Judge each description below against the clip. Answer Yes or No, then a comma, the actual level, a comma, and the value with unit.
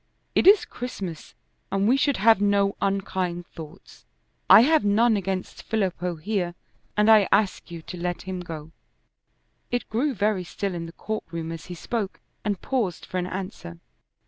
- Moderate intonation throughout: Yes, average, 3.6 semitones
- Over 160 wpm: Yes, average, 170 wpm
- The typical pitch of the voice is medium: No, high, 195 Hz